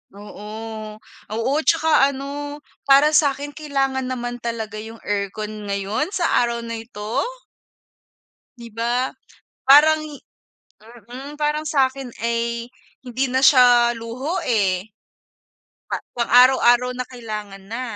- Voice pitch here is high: Yes, high, 245 Hz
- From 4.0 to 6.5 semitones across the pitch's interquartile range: No, average, 3.5 semitones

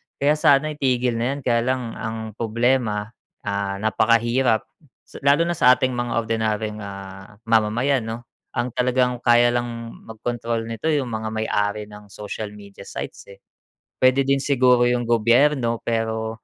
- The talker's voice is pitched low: Yes, low, 115 Hz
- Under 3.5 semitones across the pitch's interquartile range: Yes, narrow, 2.6 semitones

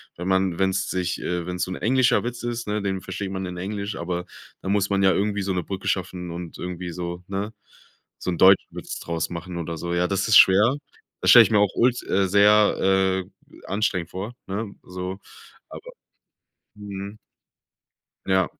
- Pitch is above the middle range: No, very low, 95 Hz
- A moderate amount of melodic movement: No, narrow, 2.2 semitones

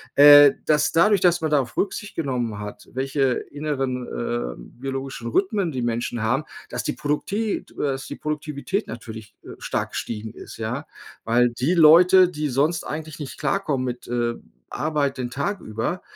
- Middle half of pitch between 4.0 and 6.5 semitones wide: Yes, average, 4.5 semitones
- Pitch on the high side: No, medium, 140 Hz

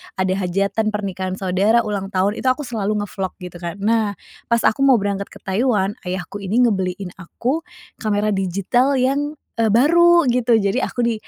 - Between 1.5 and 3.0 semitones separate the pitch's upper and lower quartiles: No, average, 3.7 semitones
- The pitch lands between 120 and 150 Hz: No, high, 205 Hz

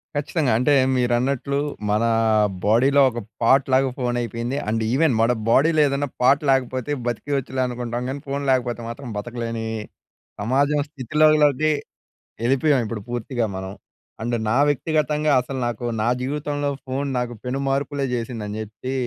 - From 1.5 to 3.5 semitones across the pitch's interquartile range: Yes, average, 3.1 semitones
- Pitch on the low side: Yes, low, 130 Hz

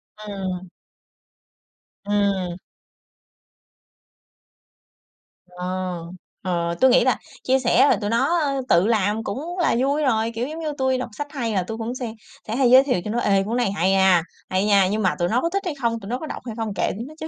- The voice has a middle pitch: No, high, 225 Hz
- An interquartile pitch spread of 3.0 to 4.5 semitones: No, average, 5.1 semitones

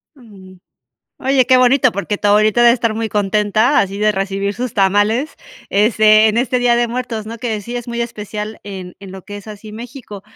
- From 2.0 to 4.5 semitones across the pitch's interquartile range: Yes, average, 2.8 semitones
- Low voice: No, high, 215 Hz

